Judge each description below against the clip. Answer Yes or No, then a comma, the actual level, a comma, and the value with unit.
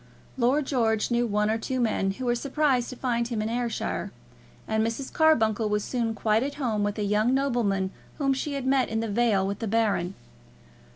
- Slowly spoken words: No, fast, 205 wpm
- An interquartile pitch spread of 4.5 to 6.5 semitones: No, average, 3.4 semitones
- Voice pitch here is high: Yes, high, 230 Hz